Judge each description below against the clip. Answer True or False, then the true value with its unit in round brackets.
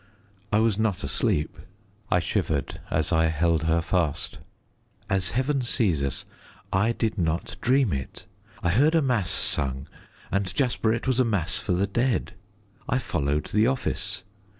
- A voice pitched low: True (95 Hz)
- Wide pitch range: True (6.4 semitones)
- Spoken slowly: False (155 wpm)